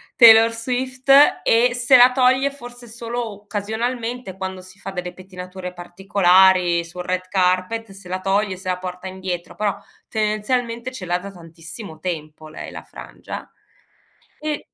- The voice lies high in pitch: Yes, high, 195 Hz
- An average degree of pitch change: Yes, average, 4.5 semitones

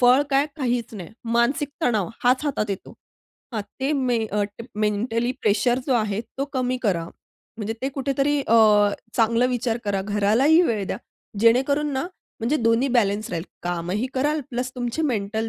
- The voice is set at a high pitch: Yes, high, 240 Hz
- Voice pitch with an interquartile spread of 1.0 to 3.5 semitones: No, average, 4.0 semitones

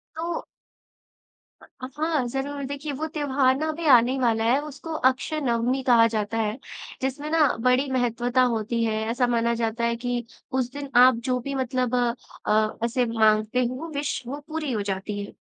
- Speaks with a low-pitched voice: No, very high, 250 Hz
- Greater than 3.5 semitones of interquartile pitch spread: No, average, 3.2 semitones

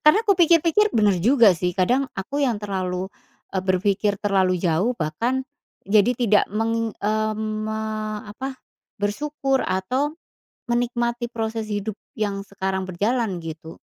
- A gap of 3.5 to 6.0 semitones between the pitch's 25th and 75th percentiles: Yes, average, 4.2 semitones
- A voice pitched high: Yes, high, 215 Hz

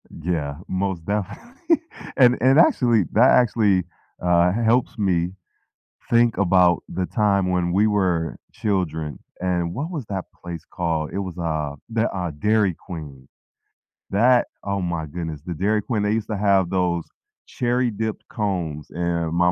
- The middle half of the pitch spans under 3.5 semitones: No, average, 4.3 semitones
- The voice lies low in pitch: Yes, very low, 95 Hz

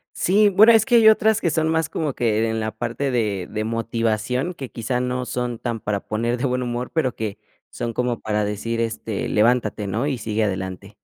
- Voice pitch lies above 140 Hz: No, low, 120 Hz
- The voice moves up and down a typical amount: Yes, average, 3.5 semitones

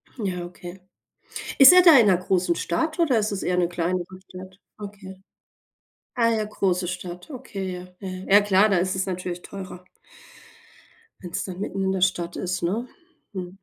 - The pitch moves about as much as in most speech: No, narrow, 2.3 semitones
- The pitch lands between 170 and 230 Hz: Yes, medium, 185 Hz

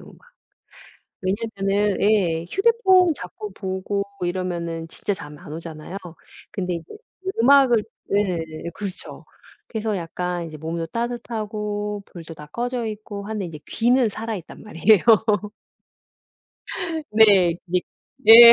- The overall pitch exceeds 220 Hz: No, high, 200 Hz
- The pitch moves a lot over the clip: No, average, 4.5 semitones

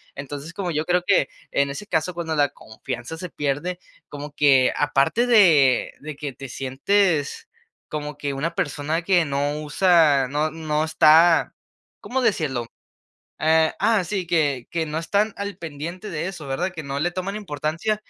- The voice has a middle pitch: Yes, medium, 155 Hz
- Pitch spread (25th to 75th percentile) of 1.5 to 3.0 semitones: No, average, 3.8 semitones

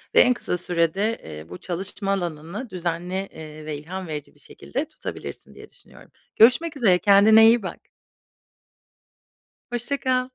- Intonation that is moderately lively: No, wide, 5.7 semitones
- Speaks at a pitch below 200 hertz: Yes, high, 190 Hz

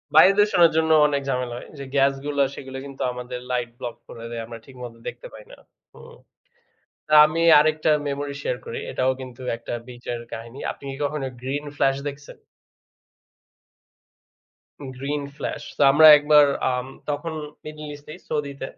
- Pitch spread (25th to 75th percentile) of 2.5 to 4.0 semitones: Yes, average, 3.0 semitones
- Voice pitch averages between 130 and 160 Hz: Yes, medium, 140 Hz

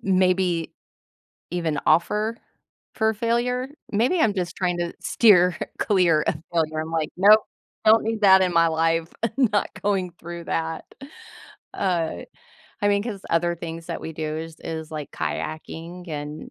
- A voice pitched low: No, medium, 175 Hz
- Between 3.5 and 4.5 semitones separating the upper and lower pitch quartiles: Yes, average, 3.9 semitones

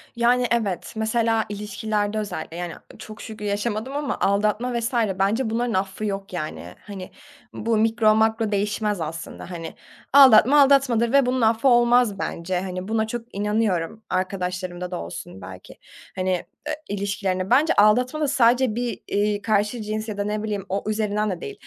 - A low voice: No, high, 215 Hz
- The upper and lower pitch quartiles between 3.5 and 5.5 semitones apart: No, average, 3.1 semitones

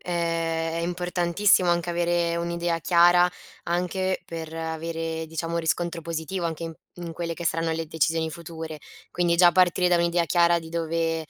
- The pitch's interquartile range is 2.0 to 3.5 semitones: No, narrow, 1.1 semitones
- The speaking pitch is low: No, medium, 170 Hz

